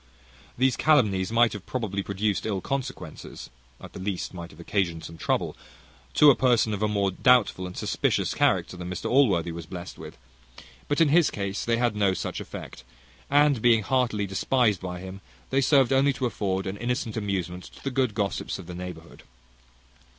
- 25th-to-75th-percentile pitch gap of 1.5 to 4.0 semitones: No, average, 5.2 semitones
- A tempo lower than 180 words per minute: No, average, 185 wpm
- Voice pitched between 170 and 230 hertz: No, low, 105 Hz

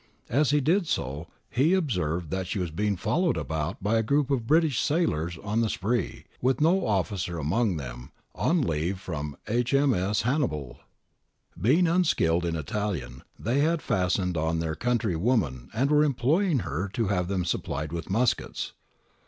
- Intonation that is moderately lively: No, wide, 8.6 semitones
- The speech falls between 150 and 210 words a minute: Yes, average, 160 wpm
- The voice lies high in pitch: No, low, 105 Hz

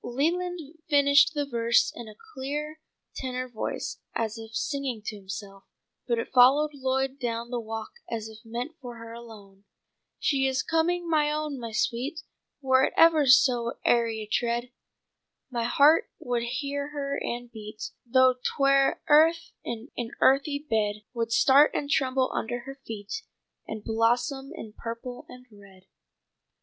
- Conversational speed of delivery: Yes, average, 155 wpm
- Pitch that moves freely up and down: No, average, 3.6 semitones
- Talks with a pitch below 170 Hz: No, very high, 250 Hz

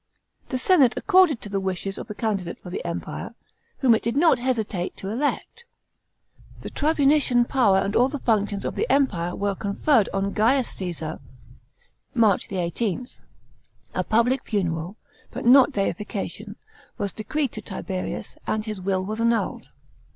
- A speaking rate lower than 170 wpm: Yes, average, 150 wpm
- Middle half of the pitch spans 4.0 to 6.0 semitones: Yes, average, 4.9 semitones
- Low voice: No, high, 215 Hz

